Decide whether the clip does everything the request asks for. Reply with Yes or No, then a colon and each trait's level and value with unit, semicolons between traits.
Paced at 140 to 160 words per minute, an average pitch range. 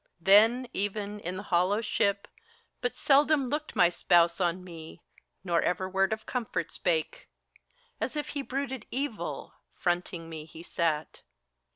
No: average, 145 wpm; wide, 5.9 semitones